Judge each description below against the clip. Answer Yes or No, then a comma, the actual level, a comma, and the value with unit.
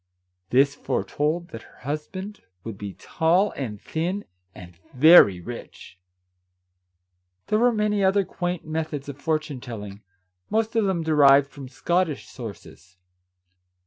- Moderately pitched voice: Yes, medium, 150 Hz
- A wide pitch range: Yes, wide, 6.7 semitones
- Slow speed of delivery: Yes, slow, 130 wpm